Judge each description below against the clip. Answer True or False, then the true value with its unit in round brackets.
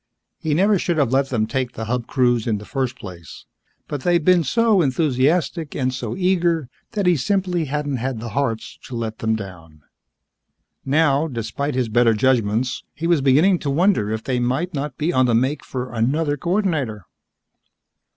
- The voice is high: False (135 Hz)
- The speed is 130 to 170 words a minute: False (180 wpm)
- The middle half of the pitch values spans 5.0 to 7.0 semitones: True (5.6 semitones)